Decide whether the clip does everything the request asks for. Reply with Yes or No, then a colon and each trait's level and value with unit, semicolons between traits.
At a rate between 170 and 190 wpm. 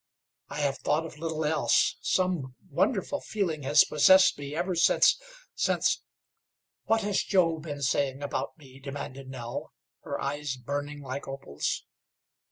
No: average, 145 wpm